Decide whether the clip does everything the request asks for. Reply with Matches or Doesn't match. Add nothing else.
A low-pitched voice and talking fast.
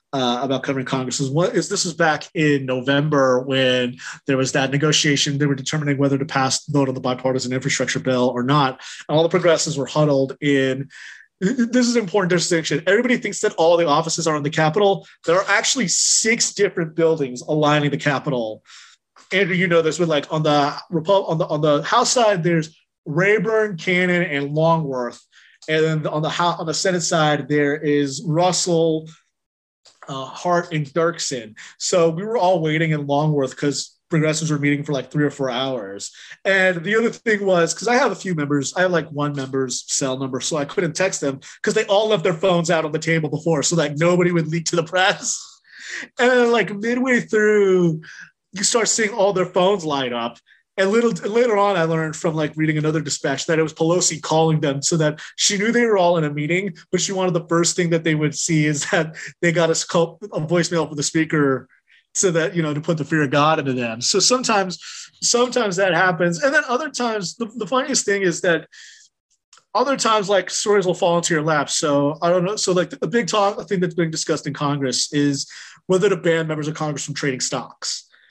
Doesn't match